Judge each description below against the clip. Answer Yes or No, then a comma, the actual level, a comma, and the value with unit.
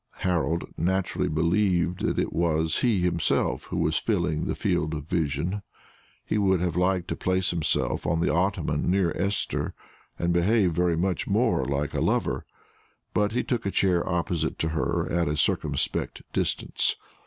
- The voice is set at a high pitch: No, very low, 85 Hz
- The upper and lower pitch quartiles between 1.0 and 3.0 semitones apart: Yes, average, 2.7 semitones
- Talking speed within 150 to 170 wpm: Yes, average, 165 wpm